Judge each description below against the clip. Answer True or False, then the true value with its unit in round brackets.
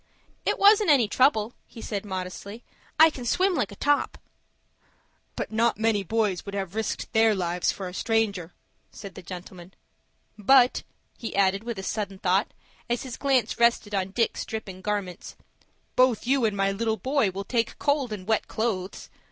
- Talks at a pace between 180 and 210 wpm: False (170 wpm)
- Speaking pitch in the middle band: False (215 Hz)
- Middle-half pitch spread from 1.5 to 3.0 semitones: False (3.6 semitones)